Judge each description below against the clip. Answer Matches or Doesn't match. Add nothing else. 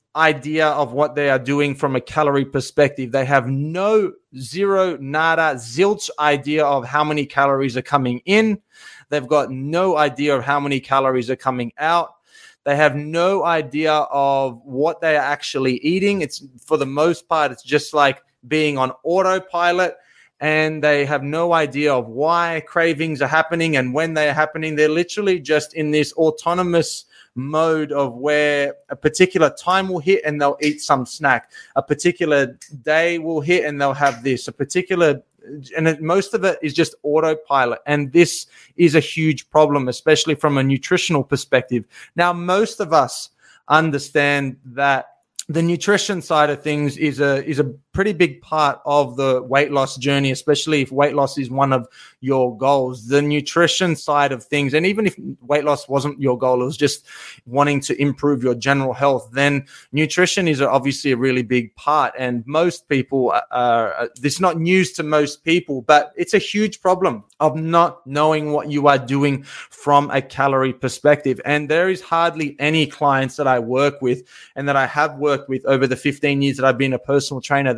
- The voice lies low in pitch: Doesn't match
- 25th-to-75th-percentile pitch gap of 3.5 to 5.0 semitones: Doesn't match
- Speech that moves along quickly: Doesn't match